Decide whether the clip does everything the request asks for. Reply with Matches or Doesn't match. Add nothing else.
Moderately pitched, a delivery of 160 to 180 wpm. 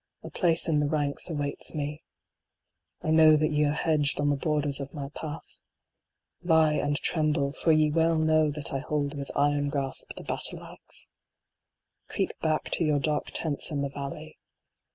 Matches